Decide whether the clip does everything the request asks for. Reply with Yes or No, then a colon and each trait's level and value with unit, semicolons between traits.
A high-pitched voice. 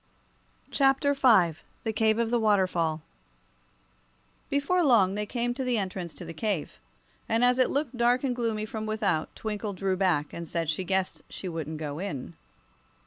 Yes: high, 210 Hz